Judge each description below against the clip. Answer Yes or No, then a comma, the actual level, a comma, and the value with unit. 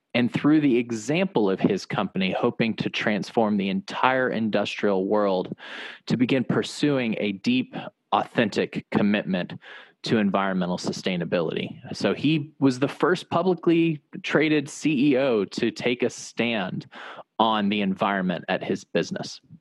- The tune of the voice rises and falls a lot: Yes, wide, 7.5 semitones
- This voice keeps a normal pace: No, slow, 130 wpm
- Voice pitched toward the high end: No, low, 135 Hz